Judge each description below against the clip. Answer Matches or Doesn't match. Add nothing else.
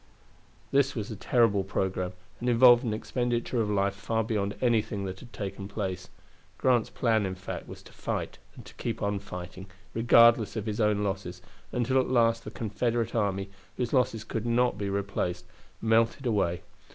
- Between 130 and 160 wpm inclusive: Doesn't match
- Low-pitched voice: Matches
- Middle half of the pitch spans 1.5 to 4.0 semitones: Matches